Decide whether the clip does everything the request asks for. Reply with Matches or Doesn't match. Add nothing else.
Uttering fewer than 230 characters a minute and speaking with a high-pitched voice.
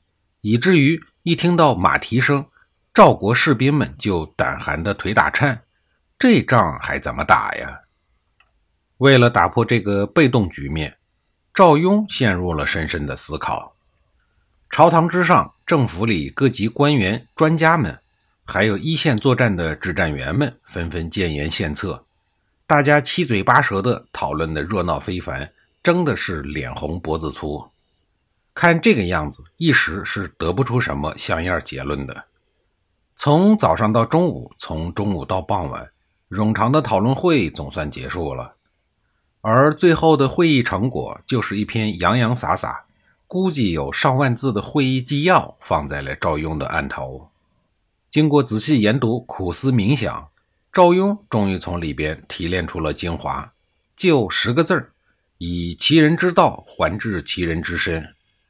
Doesn't match